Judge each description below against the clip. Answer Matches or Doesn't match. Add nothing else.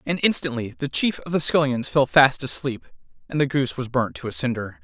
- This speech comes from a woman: Doesn't match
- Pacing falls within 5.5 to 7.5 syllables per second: Matches